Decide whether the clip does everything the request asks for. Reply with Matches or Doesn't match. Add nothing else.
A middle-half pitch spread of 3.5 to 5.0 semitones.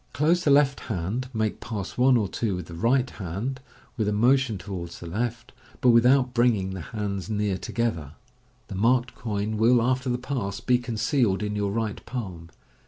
Matches